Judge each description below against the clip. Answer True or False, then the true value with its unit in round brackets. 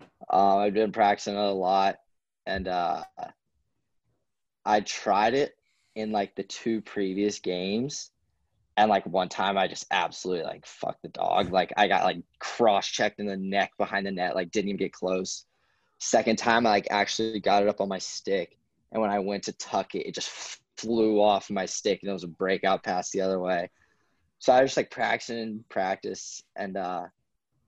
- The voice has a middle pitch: False (100 Hz)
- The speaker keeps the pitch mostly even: True (2.0 semitones)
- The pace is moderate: True (195 wpm)